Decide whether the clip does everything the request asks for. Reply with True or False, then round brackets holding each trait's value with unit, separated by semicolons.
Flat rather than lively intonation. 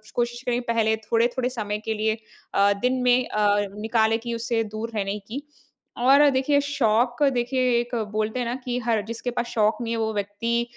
True (2.2 semitones)